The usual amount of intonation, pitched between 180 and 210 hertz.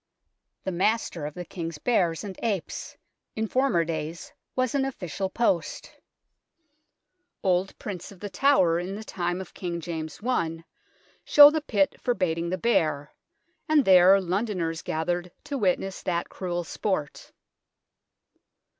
Yes: average, 4.0 semitones; medium, 185 Hz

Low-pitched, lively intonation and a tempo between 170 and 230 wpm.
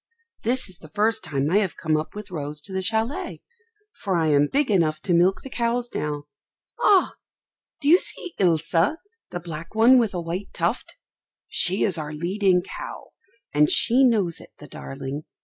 No: medium, 185 Hz; wide, 6.4 semitones; average, 185 wpm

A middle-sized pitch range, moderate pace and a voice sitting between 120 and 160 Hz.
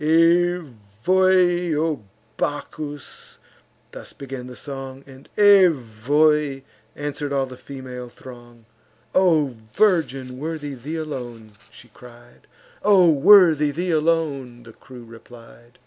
No: average, 4.7 semitones; slow, 105 wpm; medium, 140 Hz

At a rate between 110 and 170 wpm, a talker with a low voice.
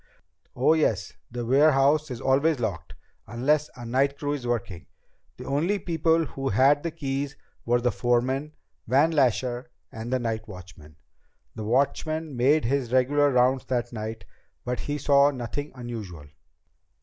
Yes: average, 145 wpm; low, 130 Hz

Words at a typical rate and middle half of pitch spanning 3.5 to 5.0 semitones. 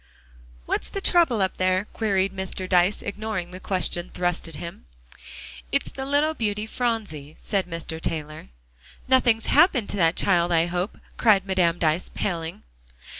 Yes: average, 150 wpm; average, 4.2 semitones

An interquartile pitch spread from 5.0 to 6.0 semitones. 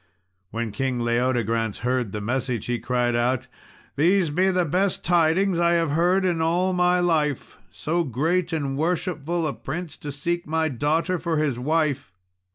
Yes: wide, 5.5 semitones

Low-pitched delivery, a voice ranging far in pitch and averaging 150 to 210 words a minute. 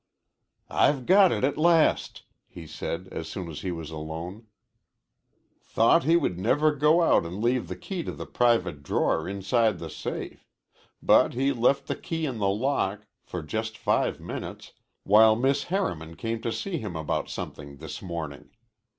Yes: low, 110 Hz; wide, 8.5 semitones; average, 170 wpm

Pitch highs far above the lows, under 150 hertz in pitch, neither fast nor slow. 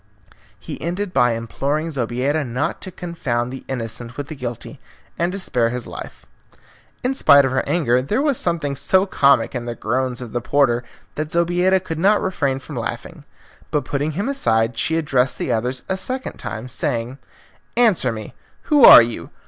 Yes: wide, 5.9 semitones; medium, 140 Hz; average, 180 wpm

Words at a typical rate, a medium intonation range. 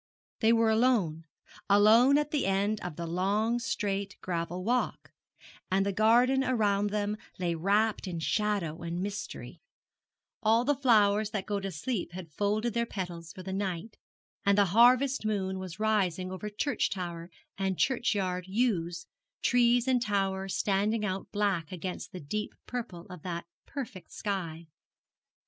Yes: average, 150 wpm; average, 3.4 semitones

